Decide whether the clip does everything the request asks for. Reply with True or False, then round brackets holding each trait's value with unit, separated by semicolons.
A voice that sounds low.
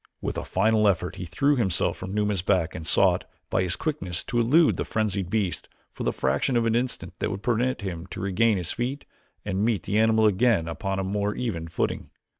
True (105 Hz)